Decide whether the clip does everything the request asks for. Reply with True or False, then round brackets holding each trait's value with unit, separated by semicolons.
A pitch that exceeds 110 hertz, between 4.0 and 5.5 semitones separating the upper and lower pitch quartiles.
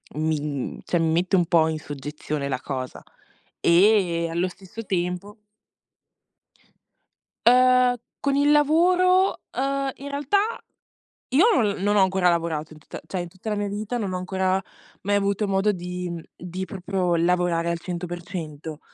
True (185 Hz; 4.3 semitones)